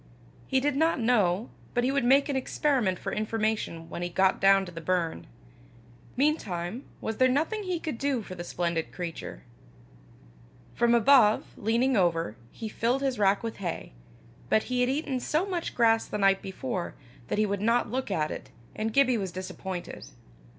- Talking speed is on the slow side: No, average, 180 wpm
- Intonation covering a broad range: Yes, wide, 5.8 semitones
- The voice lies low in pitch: No, high, 225 Hz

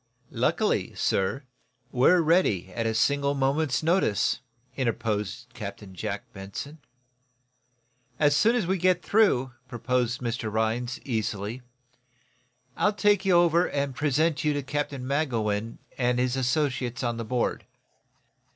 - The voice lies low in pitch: Yes, low, 130 Hz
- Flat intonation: No, average, 5.0 semitones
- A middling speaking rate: No, slow, 125 wpm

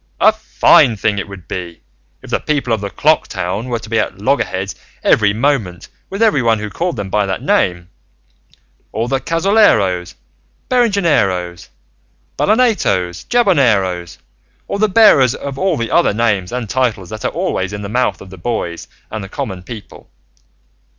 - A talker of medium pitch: No, low, 110 Hz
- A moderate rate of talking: Yes, average, 160 wpm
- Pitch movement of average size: No, wide, 6.7 semitones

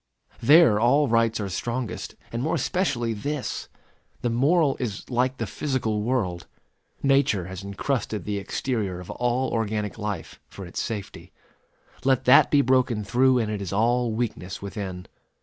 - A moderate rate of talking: Yes, average, 150 wpm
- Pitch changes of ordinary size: Yes, average, 4.1 semitones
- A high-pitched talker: No, low, 115 Hz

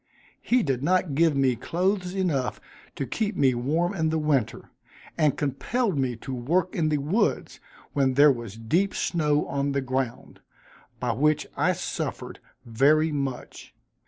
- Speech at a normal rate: Yes, average, 150 wpm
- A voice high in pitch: No, medium, 145 Hz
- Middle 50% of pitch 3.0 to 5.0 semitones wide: Yes, average, 4.4 semitones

